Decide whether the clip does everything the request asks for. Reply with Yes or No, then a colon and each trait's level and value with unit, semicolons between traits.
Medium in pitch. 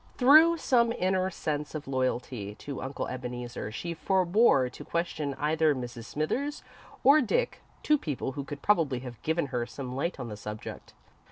Yes: medium, 145 Hz